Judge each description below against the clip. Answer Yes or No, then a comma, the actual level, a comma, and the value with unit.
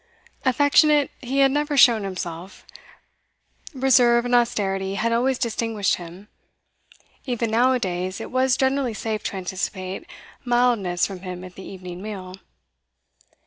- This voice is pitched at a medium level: No, high, 225 Hz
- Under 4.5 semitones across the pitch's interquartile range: No, average, 5.3 semitones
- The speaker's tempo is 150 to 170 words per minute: No, slow, 135 wpm